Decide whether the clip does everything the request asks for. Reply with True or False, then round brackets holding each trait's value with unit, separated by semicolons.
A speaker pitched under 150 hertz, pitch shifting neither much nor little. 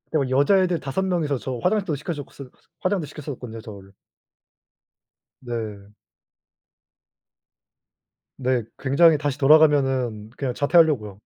True (140 Hz; 4.5 semitones)